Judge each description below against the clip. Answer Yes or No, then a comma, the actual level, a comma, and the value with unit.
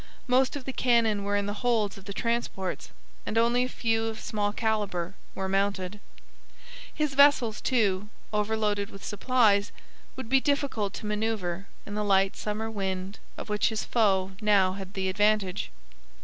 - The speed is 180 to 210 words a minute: No, average, 165 wpm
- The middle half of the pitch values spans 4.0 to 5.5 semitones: No, average, 2.7 semitones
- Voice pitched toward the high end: Yes, high, 210 Hz